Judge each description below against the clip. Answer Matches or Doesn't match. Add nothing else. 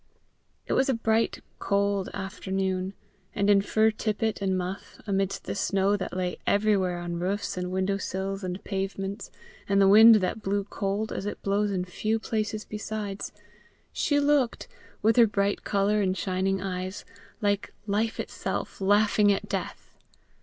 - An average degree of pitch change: Doesn't match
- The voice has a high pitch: Matches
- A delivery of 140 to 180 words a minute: Matches